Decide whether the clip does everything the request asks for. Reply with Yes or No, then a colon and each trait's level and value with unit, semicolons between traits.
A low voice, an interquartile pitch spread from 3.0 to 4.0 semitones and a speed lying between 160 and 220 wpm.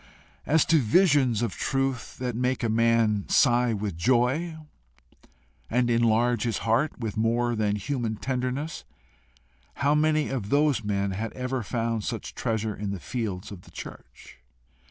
No: low, 120 Hz; average, 3.3 semitones; average, 150 wpm